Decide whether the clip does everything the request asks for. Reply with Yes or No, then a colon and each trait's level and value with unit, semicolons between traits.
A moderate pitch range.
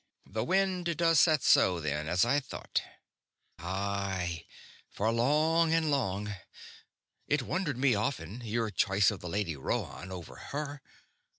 No: wide, 7.9 semitones